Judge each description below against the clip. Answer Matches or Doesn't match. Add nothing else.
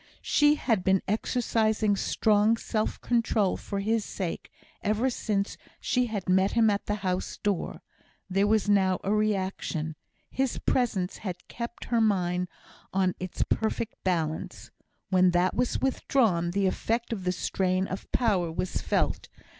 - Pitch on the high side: Matches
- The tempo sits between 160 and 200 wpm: Doesn't match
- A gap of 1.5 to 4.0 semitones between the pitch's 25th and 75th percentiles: Matches